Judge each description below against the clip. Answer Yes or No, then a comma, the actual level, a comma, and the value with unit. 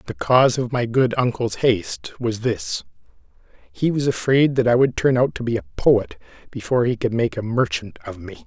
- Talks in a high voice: No, low, 120 Hz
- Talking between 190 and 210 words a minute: Yes, average, 200 wpm